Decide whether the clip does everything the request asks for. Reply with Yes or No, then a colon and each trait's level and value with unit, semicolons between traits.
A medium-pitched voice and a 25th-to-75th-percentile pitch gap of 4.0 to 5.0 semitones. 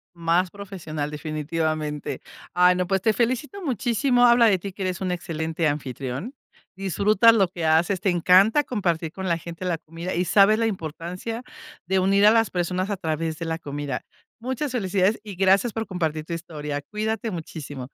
Yes: medium, 180 Hz; average, 4.4 semitones